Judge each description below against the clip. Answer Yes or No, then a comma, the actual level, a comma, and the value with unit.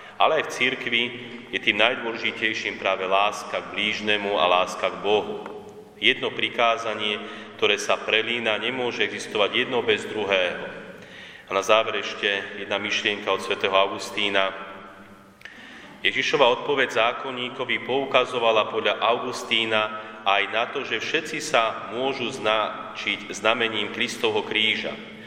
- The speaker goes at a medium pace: Yes, average, 120 wpm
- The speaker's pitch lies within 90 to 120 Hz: Yes, low, 110 Hz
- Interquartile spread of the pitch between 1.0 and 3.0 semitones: No, average, 3.4 semitones